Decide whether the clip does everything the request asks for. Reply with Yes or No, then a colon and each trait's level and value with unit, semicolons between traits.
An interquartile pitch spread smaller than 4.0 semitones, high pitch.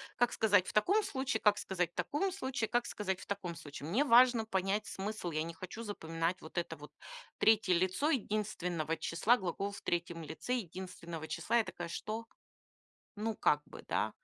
No: average, 4.9 semitones; high, 195 Hz